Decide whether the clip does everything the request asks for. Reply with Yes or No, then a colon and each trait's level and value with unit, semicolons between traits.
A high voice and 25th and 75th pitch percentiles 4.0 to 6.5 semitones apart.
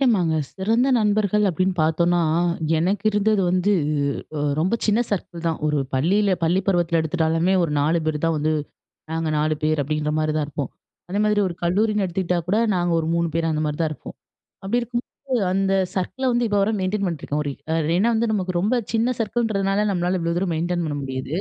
No: medium, 175 Hz; average, 4.3 semitones